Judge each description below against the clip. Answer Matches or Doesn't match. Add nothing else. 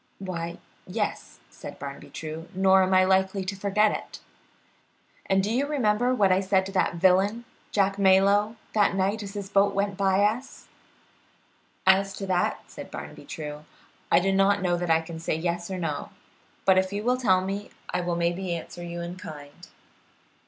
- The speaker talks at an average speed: Matches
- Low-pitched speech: Doesn't match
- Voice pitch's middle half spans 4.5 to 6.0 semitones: Doesn't match